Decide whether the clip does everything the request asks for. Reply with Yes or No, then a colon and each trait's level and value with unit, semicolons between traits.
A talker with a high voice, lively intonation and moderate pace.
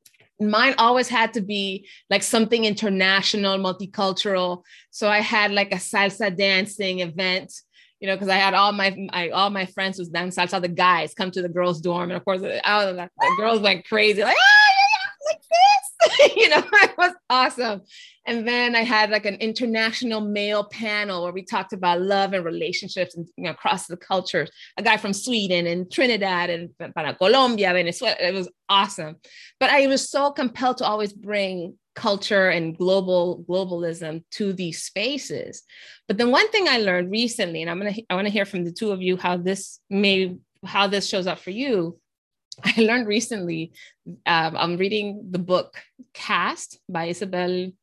No: high, 195 Hz; average, 3.6 semitones; average, 185 wpm